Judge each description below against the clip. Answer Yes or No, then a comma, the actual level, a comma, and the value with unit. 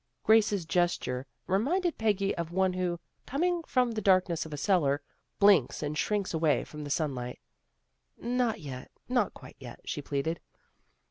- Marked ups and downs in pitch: Yes, wide, 6.2 semitones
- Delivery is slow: No, average, 155 wpm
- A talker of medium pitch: Yes, medium, 180 Hz